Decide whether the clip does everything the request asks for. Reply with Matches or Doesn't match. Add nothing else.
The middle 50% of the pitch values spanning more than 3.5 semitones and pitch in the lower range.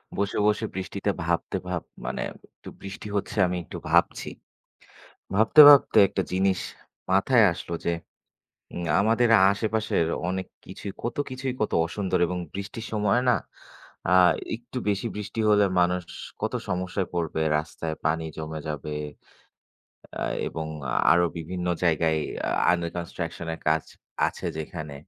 Matches